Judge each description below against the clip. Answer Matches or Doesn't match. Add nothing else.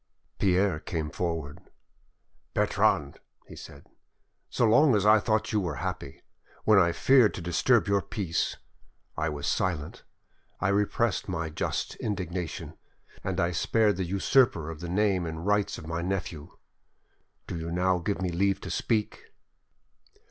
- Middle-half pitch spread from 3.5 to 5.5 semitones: Matches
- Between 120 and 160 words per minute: Matches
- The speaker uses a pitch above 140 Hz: Doesn't match